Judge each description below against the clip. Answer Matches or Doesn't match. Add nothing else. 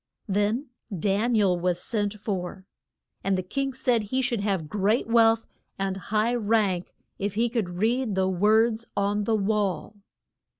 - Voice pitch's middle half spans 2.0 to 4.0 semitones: Matches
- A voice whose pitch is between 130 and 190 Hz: Doesn't match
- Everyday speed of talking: Matches